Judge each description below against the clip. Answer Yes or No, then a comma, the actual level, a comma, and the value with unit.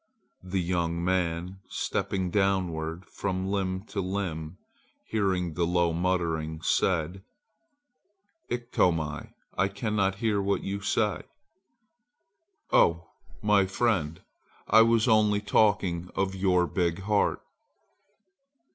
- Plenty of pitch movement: No, average, 2.8 semitones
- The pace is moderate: No, slow, 100 wpm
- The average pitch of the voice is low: Yes, very low, 95 Hz